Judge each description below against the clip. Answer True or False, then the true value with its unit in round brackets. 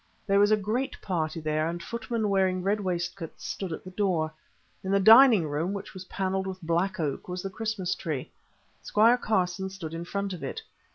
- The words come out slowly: False (195 wpm)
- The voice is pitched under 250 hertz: True (190 Hz)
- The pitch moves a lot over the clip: False (3.0 semitones)